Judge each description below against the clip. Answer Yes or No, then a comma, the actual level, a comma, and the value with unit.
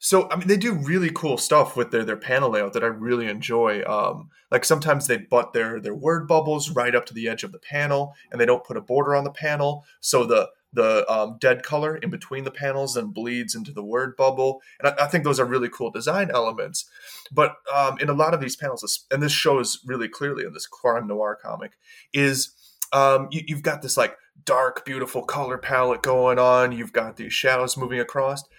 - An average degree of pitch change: Yes, average, 3.1 semitones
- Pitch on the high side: No, low, 135 Hz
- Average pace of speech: No, fast, 225 wpm